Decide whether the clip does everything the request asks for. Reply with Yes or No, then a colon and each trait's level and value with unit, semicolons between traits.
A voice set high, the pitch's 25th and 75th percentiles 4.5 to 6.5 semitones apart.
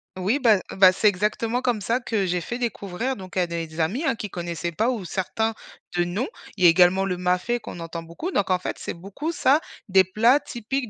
Yes: high, 195 Hz; average, 5.0 semitones